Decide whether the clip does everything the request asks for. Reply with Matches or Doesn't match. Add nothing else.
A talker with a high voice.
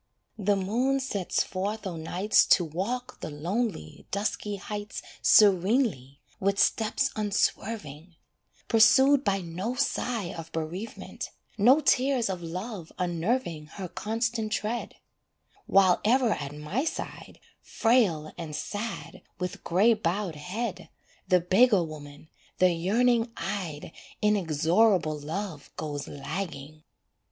Matches